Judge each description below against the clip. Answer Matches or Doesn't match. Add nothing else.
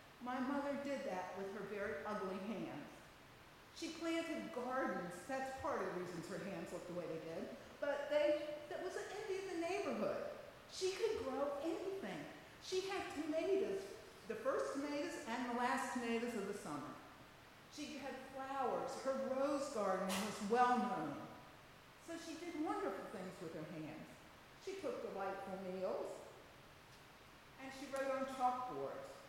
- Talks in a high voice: Matches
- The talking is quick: Doesn't match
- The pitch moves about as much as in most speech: Doesn't match